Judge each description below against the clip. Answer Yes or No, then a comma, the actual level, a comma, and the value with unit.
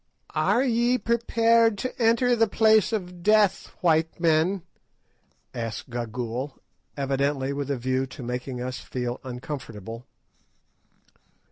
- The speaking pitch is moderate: Yes, medium, 145 Hz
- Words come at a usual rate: No, slow, 115 wpm